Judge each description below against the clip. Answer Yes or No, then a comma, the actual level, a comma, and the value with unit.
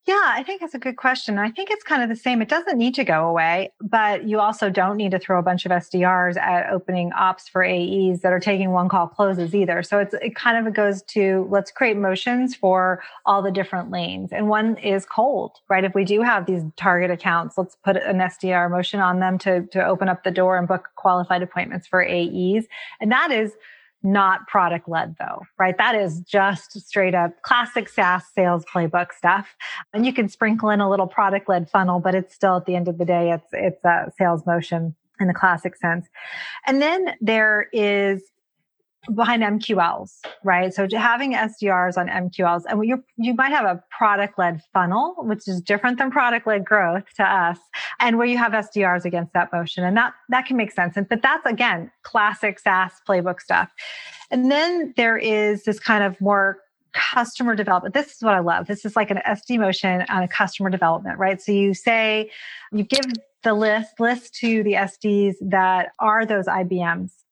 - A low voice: No, high, 195 Hz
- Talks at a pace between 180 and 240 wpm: Yes, average, 200 wpm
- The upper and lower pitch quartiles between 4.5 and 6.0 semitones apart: No, average, 3.4 semitones